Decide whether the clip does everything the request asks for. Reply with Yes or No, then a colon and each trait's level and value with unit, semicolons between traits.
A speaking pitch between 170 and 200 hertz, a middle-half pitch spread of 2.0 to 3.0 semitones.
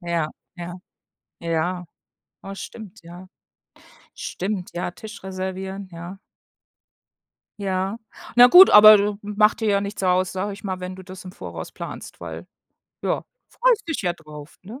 Yes: high, 190 Hz; average, 2.7 semitones